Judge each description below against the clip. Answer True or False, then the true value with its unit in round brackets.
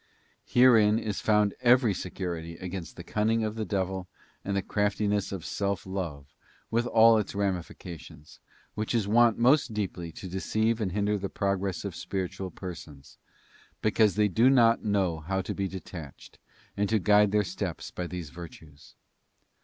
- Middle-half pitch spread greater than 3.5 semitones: False (3.1 semitones)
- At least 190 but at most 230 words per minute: False (160 wpm)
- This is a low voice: True (100 Hz)